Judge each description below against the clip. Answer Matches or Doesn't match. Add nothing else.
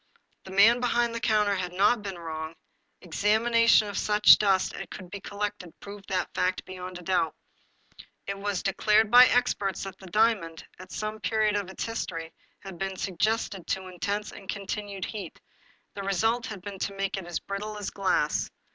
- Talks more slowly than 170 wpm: Doesn't match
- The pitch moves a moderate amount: Doesn't match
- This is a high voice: Matches